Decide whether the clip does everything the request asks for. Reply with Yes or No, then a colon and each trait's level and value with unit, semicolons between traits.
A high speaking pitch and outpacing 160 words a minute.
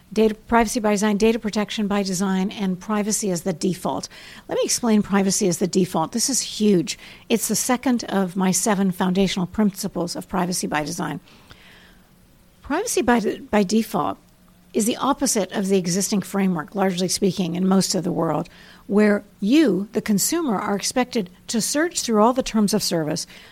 Yes: high, 200 Hz; average, 175 wpm